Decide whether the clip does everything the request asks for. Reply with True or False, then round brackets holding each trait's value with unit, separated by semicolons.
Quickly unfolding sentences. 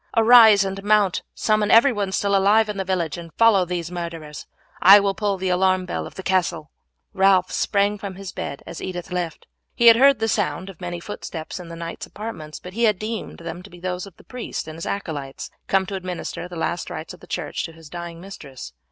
True (215 wpm)